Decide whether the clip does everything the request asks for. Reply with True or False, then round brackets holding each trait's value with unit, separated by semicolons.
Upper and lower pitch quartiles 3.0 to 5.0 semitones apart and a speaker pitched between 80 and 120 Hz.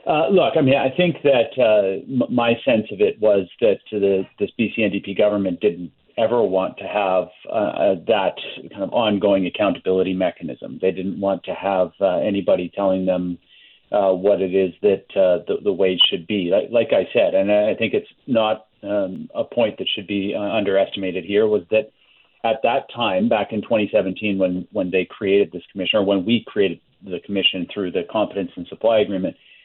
False (2.5 semitones; 100 Hz)